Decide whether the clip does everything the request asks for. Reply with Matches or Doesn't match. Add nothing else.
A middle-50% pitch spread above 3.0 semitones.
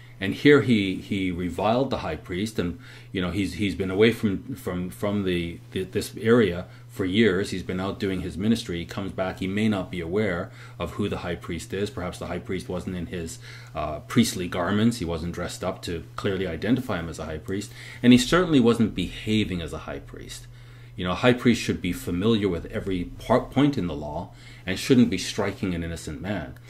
Matches